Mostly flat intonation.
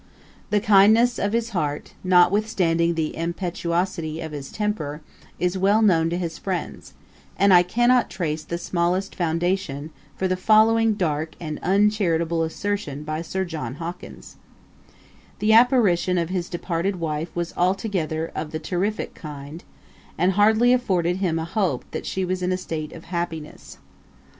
No: average, 3.5 semitones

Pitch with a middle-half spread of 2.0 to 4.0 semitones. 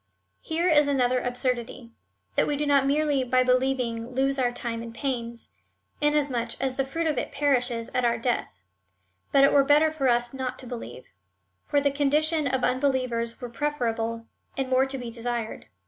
Yes: average, 2.9 semitones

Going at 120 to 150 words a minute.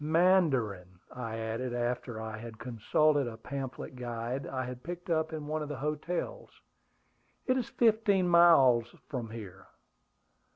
Yes: average, 140 wpm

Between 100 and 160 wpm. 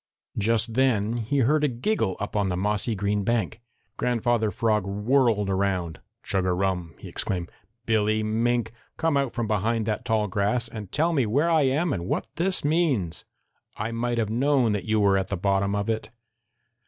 No: average, 185 wpm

